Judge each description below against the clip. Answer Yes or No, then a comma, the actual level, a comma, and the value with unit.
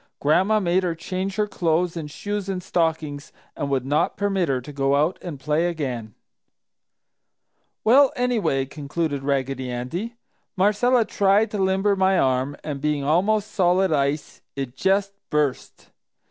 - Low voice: No, medium, 165 Hz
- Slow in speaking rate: No, average, 145 wpm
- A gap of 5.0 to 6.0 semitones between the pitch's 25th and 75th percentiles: Yes, wide, 5.5 semitones